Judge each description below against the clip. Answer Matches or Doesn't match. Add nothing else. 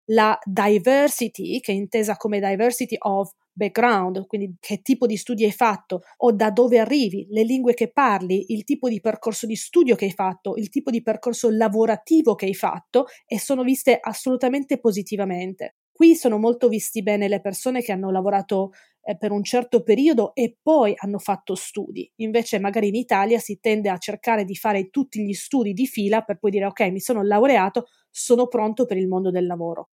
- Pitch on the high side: Matches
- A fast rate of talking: Matches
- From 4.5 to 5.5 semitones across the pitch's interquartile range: Doesn't match